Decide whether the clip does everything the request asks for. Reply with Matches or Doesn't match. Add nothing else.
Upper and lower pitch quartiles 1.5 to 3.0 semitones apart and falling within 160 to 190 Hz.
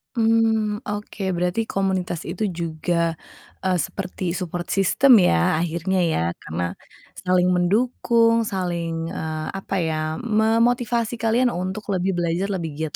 Doesn't match